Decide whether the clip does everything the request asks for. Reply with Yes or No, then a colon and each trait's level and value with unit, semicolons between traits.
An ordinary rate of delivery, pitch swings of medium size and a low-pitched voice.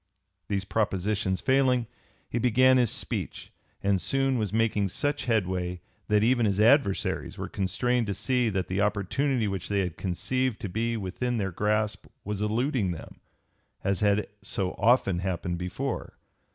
Yes: average, 150 wpm; average, 4.2 semitones; low, 105 Hz